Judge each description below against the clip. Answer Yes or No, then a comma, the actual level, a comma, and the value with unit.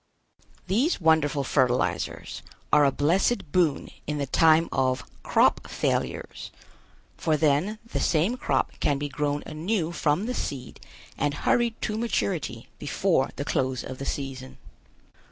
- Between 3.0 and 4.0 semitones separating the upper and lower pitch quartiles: No, average, 4.7 semitones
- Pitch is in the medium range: Yes, medium, 150 Hz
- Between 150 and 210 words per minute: No, slow, 135 wpm